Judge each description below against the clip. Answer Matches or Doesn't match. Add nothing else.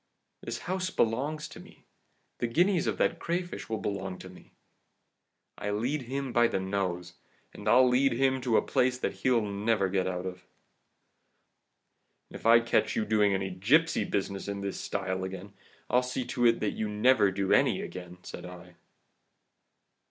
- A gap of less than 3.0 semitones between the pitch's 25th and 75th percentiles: Doesn't match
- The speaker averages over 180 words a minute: Doesn't match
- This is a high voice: Doesn't match